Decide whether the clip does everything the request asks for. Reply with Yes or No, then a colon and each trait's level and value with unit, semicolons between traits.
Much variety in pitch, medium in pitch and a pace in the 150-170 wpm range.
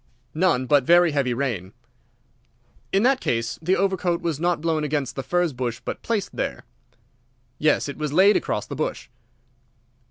No: average, 4.9 semitones; medium, 155 Hz; average, 160 wpm